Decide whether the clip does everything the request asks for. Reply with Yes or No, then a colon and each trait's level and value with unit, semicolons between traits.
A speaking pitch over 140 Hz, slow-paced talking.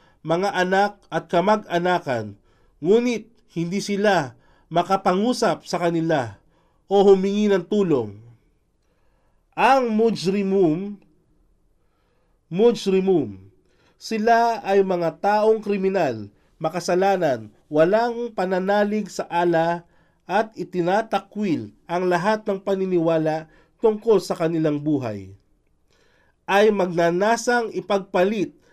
Yes: medium, 185 Hz; slow, 85 wpm